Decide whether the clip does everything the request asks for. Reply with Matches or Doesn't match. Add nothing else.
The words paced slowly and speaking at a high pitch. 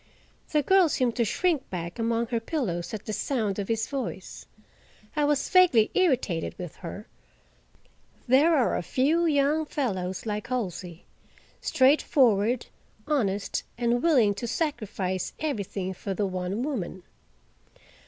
Matches